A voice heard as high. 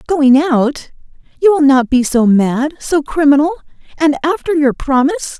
Yes: very high, 285 Hz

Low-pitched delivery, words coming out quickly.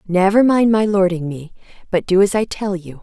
No: high, 190 Hz; fast, 220 wpm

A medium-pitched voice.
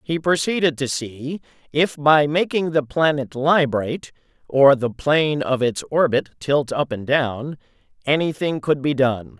Yes: medium, 145 Hz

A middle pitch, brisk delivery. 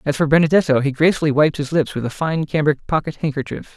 Yes: medium, 150 Hz; fast, 225 wpm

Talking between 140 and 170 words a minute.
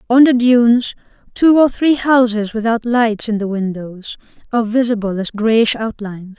Yes: average, 160 wpm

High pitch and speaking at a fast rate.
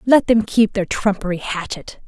No: high, 205 Hz; average, 175 wpm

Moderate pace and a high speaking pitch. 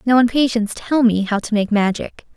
No: fast, 230 wpm; high, 225 Hz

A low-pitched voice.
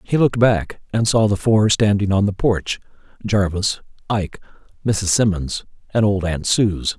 Yes: low, 100 Hz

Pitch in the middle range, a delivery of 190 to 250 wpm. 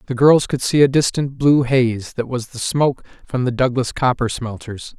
No: low, 130 Hz; fast, 205 wpm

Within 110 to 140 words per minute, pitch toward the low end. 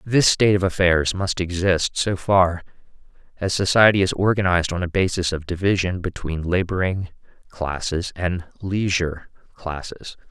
Yes: slow, 135 wpm; very low, 90 Hz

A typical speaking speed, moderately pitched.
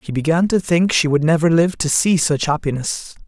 No: fast, 220 wpm; medium, 160 Hz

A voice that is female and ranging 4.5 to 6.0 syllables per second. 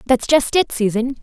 Yes: female; 4.9 syllables/s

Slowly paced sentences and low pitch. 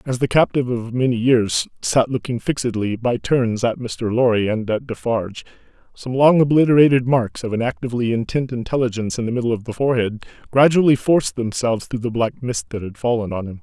No: average, 195 wpm; low, 120 Hz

